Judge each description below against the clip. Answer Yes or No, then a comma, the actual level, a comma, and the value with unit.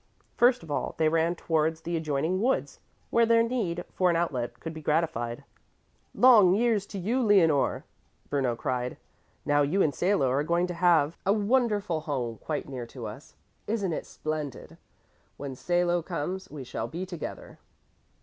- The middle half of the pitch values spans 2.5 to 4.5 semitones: No, average, 5.0 semitones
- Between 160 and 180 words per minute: Yes, average, 165 wpm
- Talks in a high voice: No, medium, 165 Hz